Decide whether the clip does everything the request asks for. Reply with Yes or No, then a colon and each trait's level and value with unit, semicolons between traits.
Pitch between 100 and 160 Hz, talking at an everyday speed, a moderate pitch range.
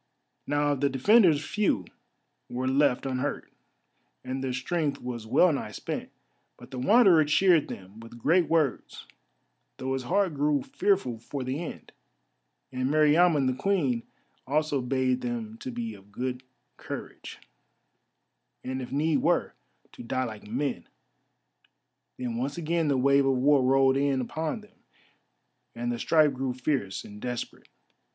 Yes: low, 135 Hz; average, 145 wpm; average, 3.4 semitones